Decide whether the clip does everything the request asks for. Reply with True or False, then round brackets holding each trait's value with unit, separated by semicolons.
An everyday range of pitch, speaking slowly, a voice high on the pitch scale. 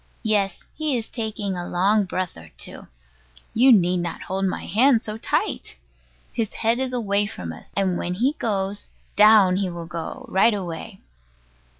False (3.6 semitones; 165 wpm; 195 Hz)